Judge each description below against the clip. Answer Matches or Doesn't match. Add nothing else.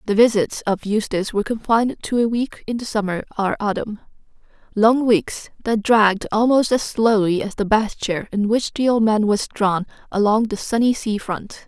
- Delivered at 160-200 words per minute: Matches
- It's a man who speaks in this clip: Doesn't match